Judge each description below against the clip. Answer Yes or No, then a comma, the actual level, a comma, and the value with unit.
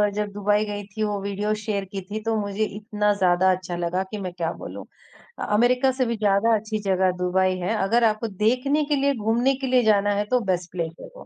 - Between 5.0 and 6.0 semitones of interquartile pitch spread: No, average, 3.1 semitones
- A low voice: No, high, 210 Hz